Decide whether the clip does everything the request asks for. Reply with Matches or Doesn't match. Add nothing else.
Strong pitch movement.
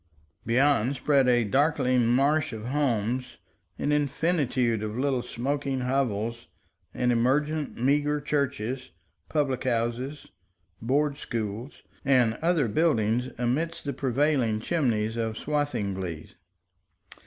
Doesn't match